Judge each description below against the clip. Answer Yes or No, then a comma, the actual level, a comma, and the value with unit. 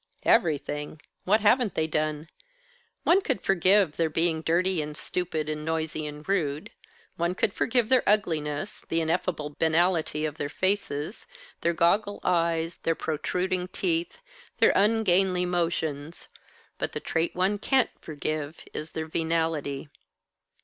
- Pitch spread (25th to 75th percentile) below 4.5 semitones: Yes, average, 3.3 semitones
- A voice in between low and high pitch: Yes, medium, 165 Hz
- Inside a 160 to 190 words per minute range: No, slow, 135 wpm